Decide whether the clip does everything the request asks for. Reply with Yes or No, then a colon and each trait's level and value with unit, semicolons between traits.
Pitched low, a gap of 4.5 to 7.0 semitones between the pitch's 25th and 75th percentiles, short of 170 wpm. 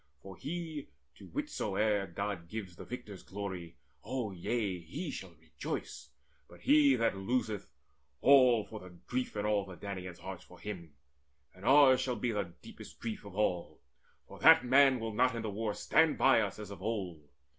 No: low, 105 Hz; average, 4.9 semitones; average, 175 wpm